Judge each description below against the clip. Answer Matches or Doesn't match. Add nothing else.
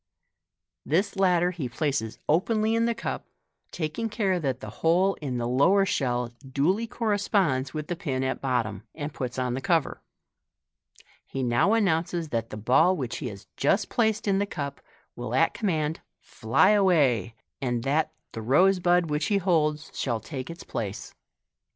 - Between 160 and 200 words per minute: Matches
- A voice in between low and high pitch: Matches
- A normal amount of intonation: Doesn't match